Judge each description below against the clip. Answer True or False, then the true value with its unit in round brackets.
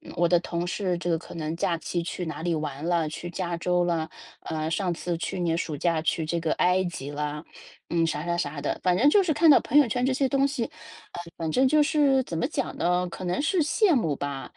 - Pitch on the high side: False (175 Hz)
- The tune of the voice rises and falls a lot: True (7.1 semitones)